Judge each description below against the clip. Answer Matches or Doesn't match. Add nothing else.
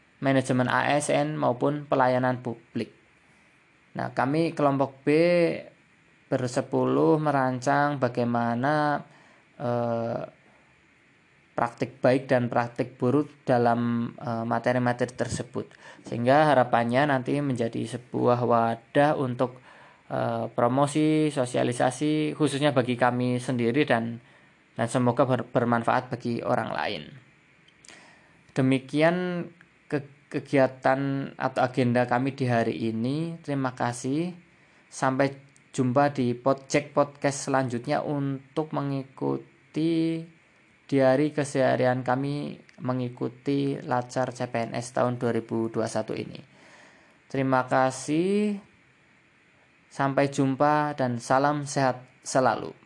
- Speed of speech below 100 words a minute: Matches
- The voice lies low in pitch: Matches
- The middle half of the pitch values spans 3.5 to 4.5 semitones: Doesn't match